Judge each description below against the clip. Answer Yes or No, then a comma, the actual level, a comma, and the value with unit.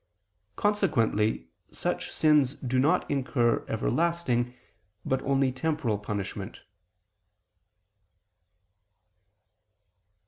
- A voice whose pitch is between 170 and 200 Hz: No, low, 130 Hz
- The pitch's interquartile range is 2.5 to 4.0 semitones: No, average, 4.9 semitones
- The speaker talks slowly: Yes, slow, 65 wpm